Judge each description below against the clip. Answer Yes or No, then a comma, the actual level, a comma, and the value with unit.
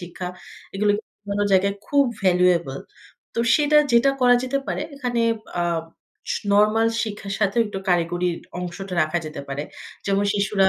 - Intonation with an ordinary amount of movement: Yes, average, 4.0 semitones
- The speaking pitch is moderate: No, high, 200 Hz